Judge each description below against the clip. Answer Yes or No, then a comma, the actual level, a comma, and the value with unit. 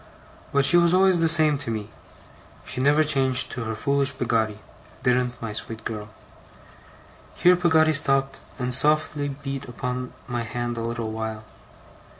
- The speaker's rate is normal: Yes, average, 155 wpm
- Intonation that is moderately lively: Yes, average, 4.3 semitones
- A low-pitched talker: Yes, low, 130 Hz